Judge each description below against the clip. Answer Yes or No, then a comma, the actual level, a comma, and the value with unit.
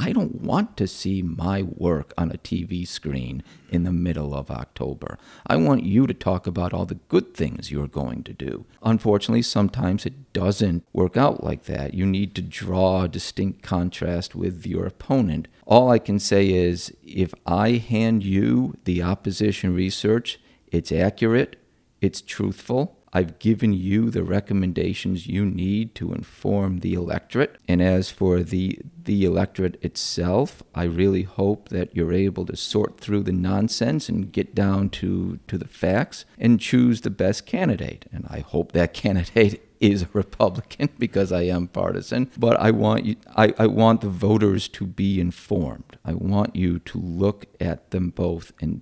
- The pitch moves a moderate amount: Yes, average, 3.2 semitones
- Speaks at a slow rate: No, average, 170 wpm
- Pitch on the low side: Yes, very low, 95 Hz